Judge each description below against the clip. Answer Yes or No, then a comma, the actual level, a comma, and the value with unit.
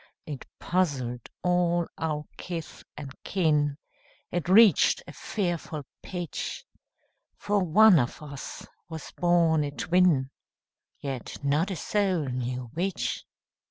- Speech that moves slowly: Yes, slow, 115 wpm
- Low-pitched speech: No, medium, 160 Hz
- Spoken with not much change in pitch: No, average, 4.1 semitones